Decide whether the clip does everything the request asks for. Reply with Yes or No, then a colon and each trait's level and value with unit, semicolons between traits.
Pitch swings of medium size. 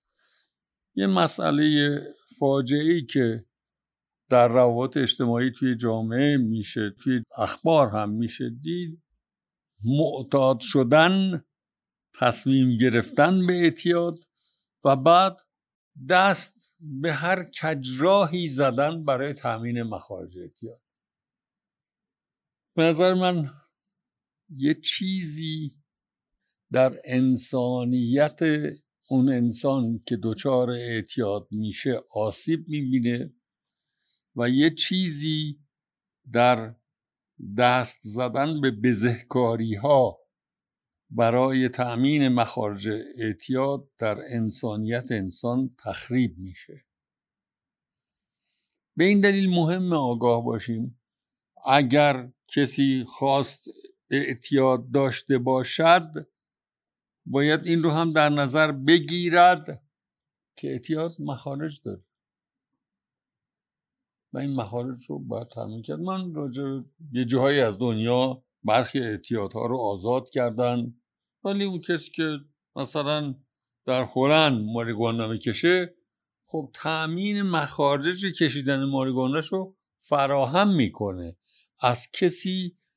Yes: average, 4.7 semitones